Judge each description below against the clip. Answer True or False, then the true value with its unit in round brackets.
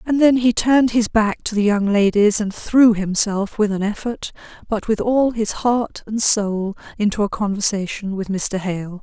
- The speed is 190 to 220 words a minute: True (195 wpm)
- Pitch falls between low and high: False (215 Hz)